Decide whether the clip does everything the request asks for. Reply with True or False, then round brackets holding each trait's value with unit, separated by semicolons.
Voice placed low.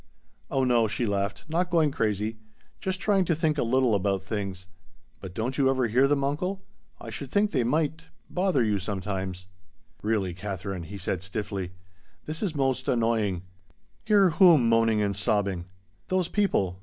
True (115 Hz)